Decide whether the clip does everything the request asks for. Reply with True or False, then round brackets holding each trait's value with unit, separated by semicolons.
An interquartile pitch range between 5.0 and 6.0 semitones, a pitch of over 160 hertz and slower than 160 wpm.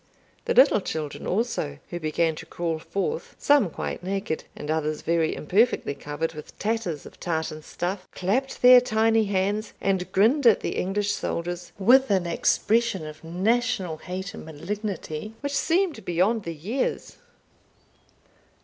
True (5.5 semitones; 190 Hz; 145 wpm)